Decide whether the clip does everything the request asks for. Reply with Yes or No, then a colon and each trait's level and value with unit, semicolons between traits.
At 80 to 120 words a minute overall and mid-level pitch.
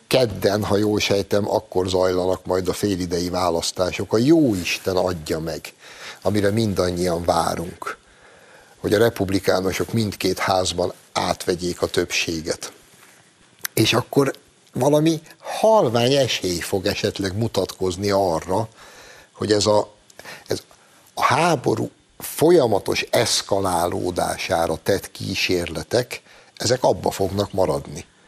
No: slow, 105 wpm; very low, 95 Hz